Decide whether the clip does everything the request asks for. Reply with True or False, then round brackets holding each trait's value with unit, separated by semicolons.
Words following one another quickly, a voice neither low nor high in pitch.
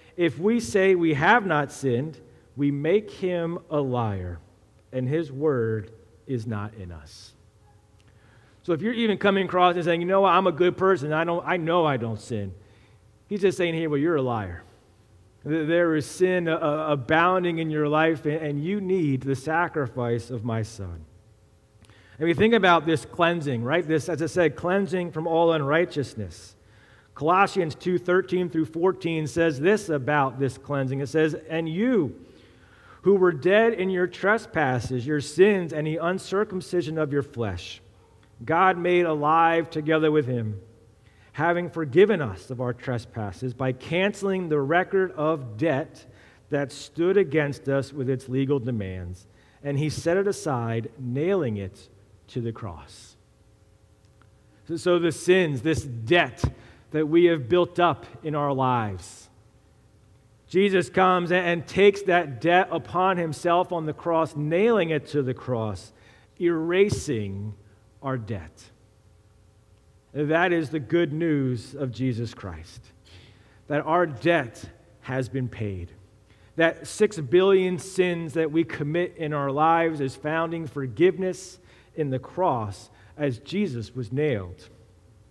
False (145 wpm; 145 Hz)